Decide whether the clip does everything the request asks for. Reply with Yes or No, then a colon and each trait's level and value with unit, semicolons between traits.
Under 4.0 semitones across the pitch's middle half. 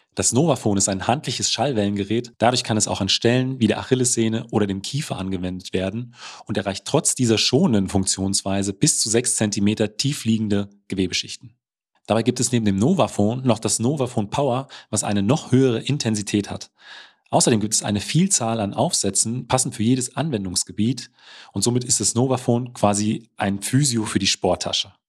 Yes: average, 3.6 semitones